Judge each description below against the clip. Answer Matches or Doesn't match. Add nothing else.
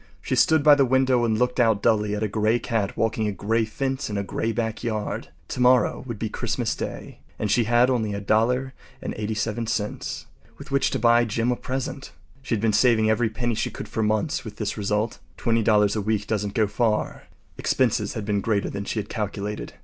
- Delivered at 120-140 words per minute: Doesn't match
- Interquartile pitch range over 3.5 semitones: Doesn't match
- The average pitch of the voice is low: Matches